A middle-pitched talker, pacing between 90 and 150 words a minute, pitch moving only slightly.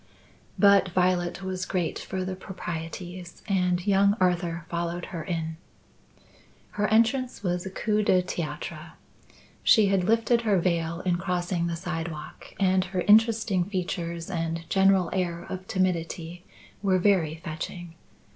Yes: medium, 180 Hz; slow, 135 wpm; narrow, 2.1 semitones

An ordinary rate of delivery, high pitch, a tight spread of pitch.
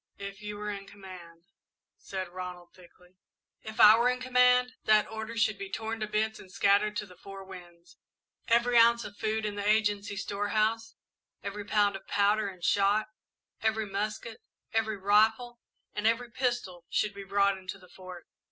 Yes: average, 175 wpm; high, 210 Hz; narrow, 2.1 semitones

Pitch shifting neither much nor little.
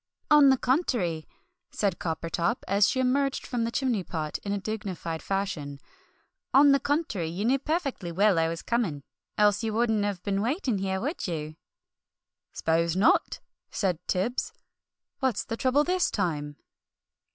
No: wide, 7.0 semitones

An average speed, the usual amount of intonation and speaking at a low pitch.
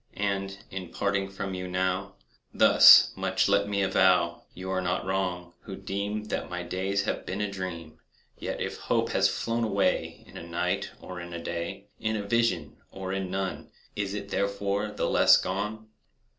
No: average, 180 wpm; narrow, 1.6 semitones; very low, 95 Hz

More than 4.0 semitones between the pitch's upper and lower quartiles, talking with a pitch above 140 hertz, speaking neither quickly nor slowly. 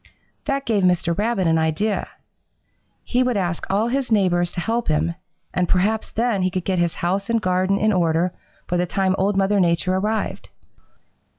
No: average, 3.6 semitones; high, 190 Hz; average, 180 wpm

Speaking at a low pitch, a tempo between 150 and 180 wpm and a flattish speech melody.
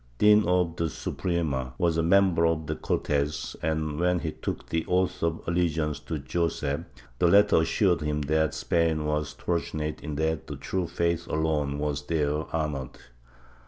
Yes: very low, 80 Hz; average, 160 wpm; narrow, 2.2 semitones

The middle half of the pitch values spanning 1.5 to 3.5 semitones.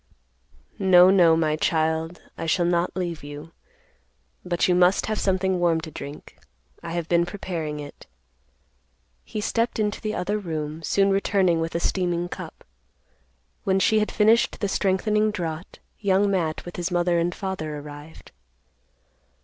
Yes: average, 3.0 semitones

